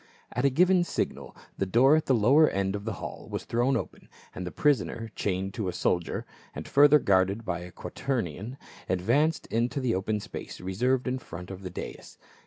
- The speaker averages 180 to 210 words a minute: Yes, average, 195 wpm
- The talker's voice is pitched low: Yes, low, 115 Hz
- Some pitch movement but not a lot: No, wide, 6.1 semitones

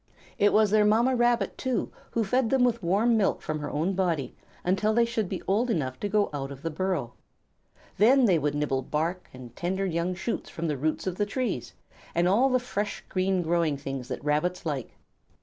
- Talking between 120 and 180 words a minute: No, fast, 205 wpm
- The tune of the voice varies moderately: No, wide, 6.1 semitones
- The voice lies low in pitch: No, medium, 185 Hz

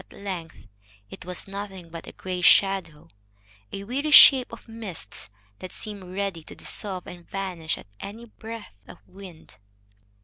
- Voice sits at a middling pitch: No, high, 195 Hz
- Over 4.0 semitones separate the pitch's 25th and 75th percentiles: No, average, 2.7 semitones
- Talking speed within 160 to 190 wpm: No, average, 150 wpm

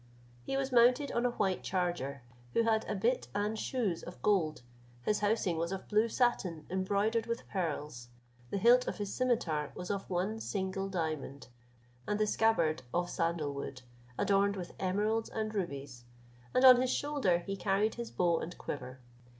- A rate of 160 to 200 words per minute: Yes, average, 170 wpm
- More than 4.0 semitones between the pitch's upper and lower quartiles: Yes, average, 4.8 semitones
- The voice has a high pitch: Yes, high, 195 Hz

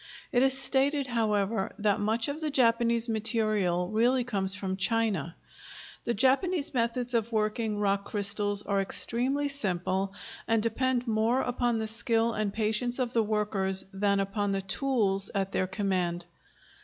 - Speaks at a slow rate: No, average, 150 wpm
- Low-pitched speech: No, high, 220 Hz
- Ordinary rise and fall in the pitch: Yes, average, 3.4 semitones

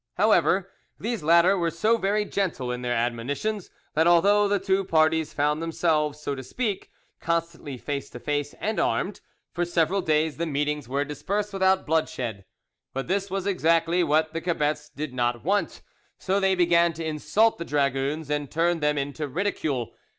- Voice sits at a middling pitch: Yes, medium, 160 Hz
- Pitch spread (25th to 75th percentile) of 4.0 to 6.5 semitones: Yes, average, 4.4 semitones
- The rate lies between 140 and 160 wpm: No, average, 170 wpm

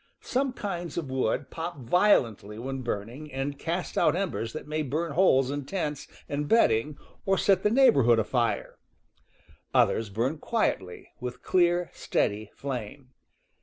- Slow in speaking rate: No, average, 145 wpm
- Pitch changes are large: Yes, wide, 6.4 semitones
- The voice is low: No, medium, 145 Hz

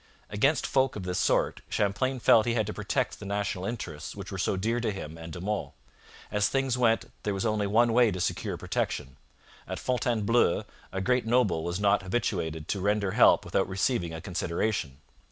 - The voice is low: Yes, low, 105 Hz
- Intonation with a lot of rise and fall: No, average, 4.1 semitones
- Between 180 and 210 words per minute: Yes, average, 195 wpm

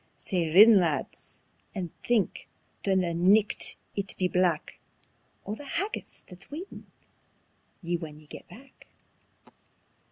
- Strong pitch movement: No, average, 4.2 semitones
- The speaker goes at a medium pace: No, slow, 125 wpm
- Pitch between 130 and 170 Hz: No, high, 190 Hz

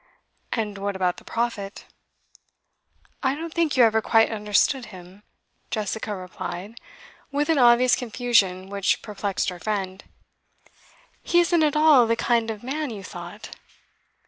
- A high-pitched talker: Yes, high, 220 Hz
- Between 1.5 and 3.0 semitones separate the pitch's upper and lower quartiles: No, average, 4.4 semitones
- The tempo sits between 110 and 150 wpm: Yes, average, 140 wpm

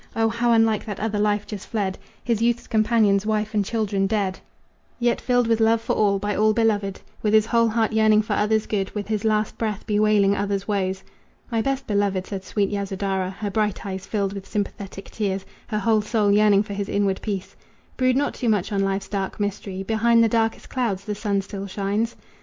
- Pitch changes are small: Yes, narrow, 2.0 semitones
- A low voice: No, high, 210 Hz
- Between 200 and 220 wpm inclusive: Yes, fast, 205 wpm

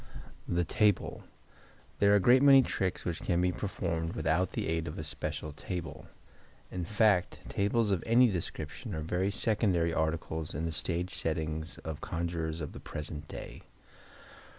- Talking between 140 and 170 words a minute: Yes, average, 155 wpm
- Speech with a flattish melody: No, average, 3.9 semitones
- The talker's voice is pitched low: Yes, very low, 85 Hz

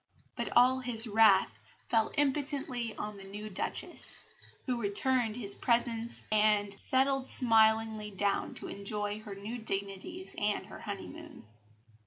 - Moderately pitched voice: No, high, 220 Hz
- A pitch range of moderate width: Yes, average, 3.3 semitones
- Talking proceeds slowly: Yes, slow, 130 wpm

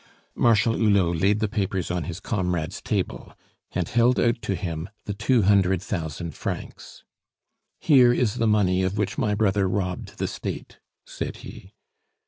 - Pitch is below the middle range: Yes, low, 100 Hz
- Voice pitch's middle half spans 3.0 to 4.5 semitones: Yes, average, 3.3 semitones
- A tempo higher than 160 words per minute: No, average, 155 wpm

